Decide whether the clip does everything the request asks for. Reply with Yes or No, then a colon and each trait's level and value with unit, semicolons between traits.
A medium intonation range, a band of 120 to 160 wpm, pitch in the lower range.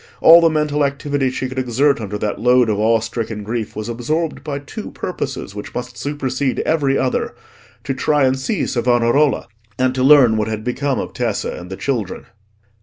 No: average, 3.8 semitones; average, 185 wpm; low, 130 Hz